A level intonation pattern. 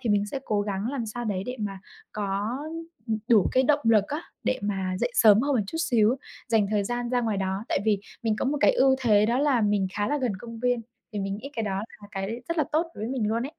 No: average, 3.7 semitones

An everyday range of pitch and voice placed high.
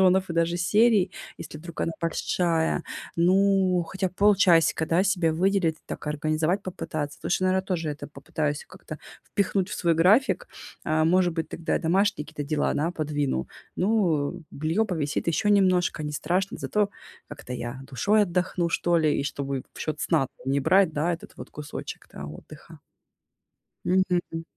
No: average, 3.4 semitones; medium, 170 Hz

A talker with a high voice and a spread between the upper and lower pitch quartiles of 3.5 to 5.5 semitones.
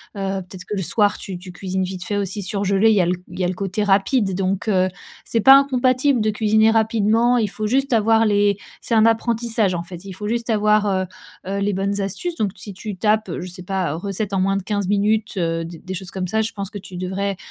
No: high, 200 Hz; narrow, 2.6 semitones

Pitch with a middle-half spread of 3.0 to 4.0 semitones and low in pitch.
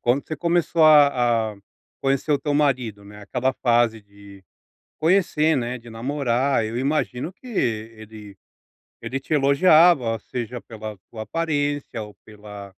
No: average, 4.9 semitones; low, 125 Hz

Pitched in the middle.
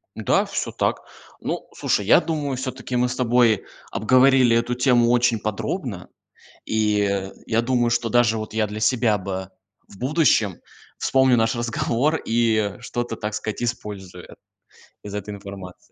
No: low, 115 Hz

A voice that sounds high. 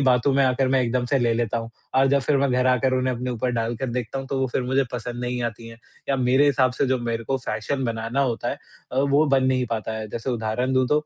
No: low, 125 Hz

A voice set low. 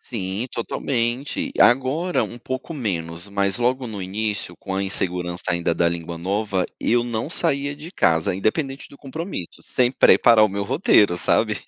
Yes: low, 110 Hz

